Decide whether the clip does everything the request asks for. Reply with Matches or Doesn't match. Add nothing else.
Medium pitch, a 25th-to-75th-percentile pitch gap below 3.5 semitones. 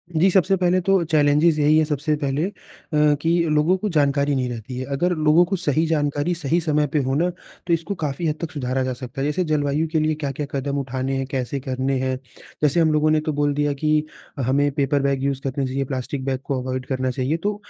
Matches